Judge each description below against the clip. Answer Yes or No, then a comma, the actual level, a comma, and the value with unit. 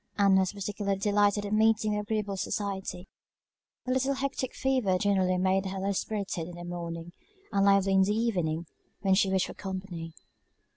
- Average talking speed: Yes, average, 175 wpm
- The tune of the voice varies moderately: No, narrow, 1.8 semitones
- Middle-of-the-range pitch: No, high, 195 Hz